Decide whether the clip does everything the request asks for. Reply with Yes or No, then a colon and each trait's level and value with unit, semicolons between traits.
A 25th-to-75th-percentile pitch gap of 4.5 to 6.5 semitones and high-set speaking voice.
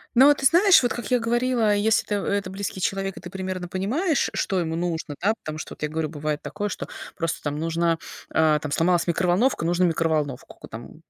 No: average, 5.1 semitones; medium, 180 Hz